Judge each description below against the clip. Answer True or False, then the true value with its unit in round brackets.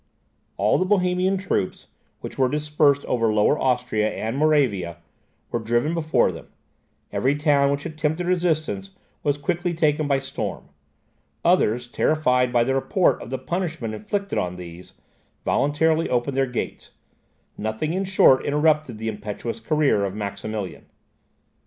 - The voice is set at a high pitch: False (140 Hz)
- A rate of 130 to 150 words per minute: True (140 wpm)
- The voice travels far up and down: True (5.7 semitones)